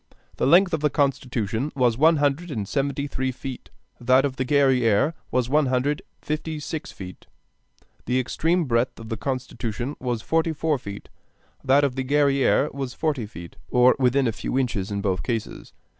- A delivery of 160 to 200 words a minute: Yes, average, 180 wpm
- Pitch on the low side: Yes, low, 130 Hz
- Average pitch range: Yes, average, 3.4 semitones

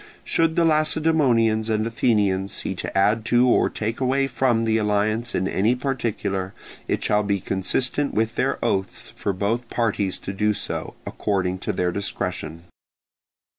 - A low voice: Yes, low, 110 Hz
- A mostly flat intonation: No, average, 3.8 semitones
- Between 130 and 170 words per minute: Yes, average, 155 wpm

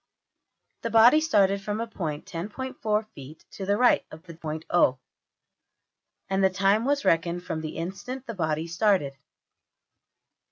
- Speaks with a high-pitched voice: Yes, high, 195 Hz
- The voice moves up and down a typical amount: Yes, average, 5.0 semitones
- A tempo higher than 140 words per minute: No, slow, 135 wpm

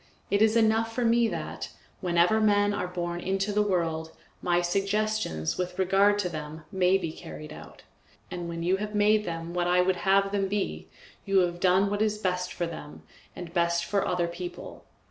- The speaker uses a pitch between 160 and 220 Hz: Yes, medium, 185 Hz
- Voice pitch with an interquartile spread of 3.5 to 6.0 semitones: No, average, 3.0 semitones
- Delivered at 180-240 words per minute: Yes, average, 190 wpm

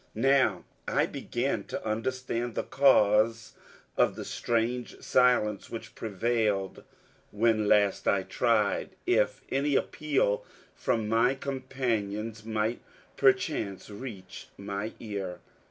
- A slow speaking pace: Yes, slow, 105 wpm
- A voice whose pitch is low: Yes, low, 115 Hz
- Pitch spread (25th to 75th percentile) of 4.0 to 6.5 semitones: No, average, 3.4 semitones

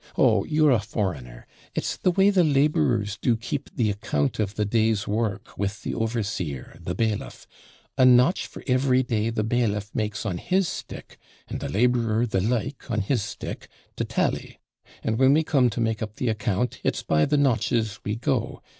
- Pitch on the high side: No, low, 115 Hz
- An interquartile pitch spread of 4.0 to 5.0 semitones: No, average, 3.5 semitones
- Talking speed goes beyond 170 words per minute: Yes, average, 185 wpm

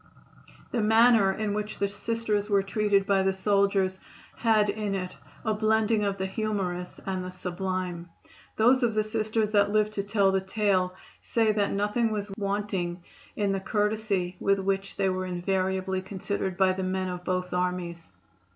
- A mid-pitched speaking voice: No, high, 195 Hz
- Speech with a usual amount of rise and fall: No, narrow, 2.2 semitones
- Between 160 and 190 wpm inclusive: Yes, average, 170 wpm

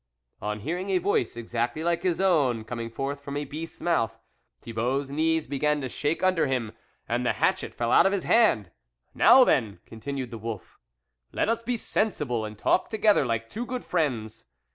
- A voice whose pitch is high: No, medium, 140 Hz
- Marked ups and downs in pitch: Yes, wide, 7.1 semitones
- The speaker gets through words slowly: No, average, 190 wpm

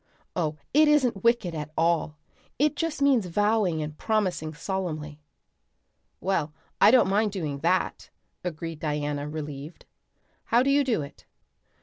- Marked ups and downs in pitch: Yes, wide, 6.6 semitones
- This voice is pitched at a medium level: Yes, medium, 175 Hz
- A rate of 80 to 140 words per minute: Yes, slow, 135 wpm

